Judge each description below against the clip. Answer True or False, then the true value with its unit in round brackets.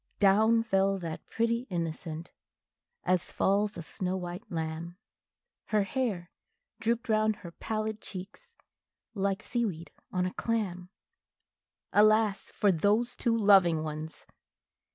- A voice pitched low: False (195 Hz)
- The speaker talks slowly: True (120 wpm)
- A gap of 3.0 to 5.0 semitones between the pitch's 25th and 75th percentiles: True (3.9 semitones)